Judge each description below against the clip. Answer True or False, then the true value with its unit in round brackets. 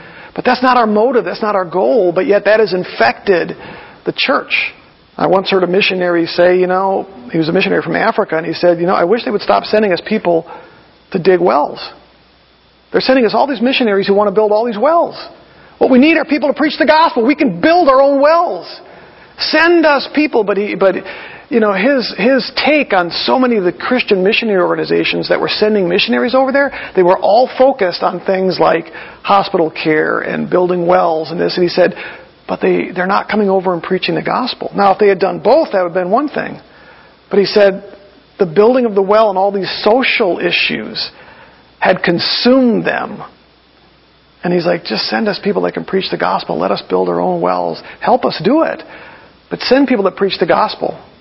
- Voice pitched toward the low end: False (200 Hz)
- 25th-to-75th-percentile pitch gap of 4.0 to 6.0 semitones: True (5.4 semitones)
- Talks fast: True (215 wpm)